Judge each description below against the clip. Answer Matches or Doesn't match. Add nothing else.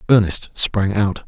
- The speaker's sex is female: Doesn't match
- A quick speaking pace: Doesn't match